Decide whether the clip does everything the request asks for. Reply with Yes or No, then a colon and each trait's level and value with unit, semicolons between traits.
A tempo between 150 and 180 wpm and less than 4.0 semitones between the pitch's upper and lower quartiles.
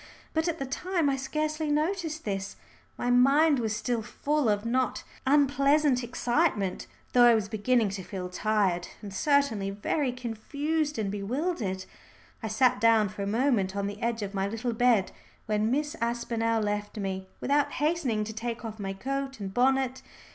No: average, 170 wpm; average, 5.3 semitones